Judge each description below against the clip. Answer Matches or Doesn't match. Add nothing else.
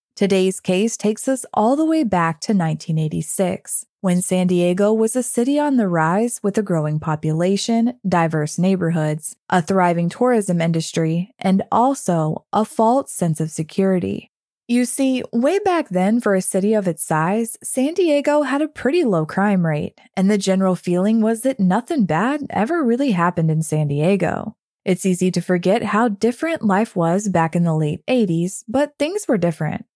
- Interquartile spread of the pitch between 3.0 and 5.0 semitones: Doesn't match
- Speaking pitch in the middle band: Doesn't match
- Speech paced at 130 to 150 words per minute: Doesn't match